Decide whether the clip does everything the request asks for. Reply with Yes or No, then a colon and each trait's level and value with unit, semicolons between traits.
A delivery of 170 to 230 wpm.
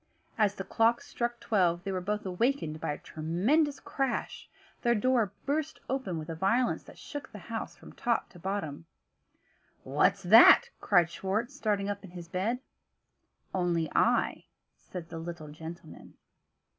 No: average, 155 wpm